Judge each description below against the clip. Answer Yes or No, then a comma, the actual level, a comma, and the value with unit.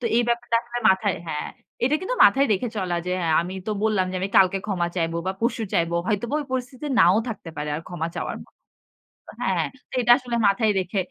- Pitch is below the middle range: No, high, 205 Hz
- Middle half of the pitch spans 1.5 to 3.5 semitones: No, average, 4.9 semitones